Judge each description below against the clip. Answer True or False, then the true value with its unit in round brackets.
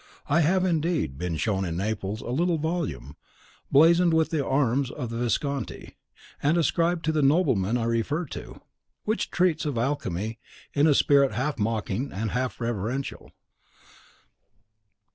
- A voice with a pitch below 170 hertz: True (135 Hz)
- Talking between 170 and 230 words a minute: False (145 wpm)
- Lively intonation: True (6.1 semitones)